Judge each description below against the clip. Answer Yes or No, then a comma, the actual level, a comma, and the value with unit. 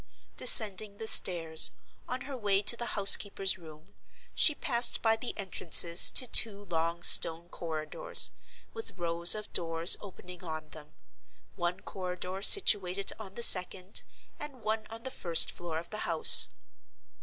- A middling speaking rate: Yes, average, 150 wpm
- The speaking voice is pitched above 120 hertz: Yes, high, 190 Hz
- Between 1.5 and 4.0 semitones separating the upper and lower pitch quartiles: No, average, 4.5 semitones